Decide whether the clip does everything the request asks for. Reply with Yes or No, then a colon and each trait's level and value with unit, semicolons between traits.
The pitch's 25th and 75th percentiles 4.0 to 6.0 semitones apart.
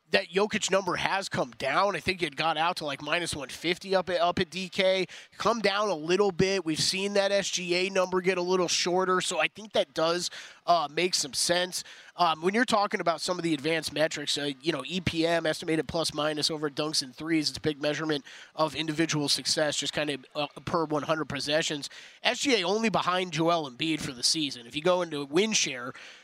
No: average, 3.3 semitones